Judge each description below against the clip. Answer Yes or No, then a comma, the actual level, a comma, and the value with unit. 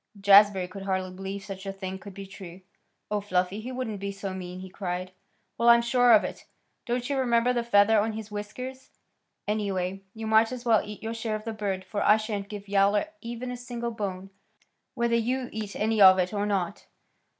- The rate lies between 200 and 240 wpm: Yes, fast, 205 wpm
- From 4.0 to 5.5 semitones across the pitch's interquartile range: No, average, 3.1 semitones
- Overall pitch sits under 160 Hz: No, high, 210 Hz